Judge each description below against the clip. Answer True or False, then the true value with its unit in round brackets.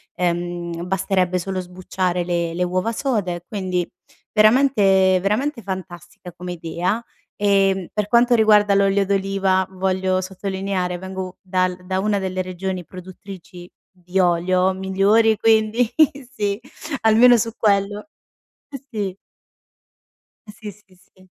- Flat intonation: True (2.2 semitones)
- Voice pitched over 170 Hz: True (190 Hz)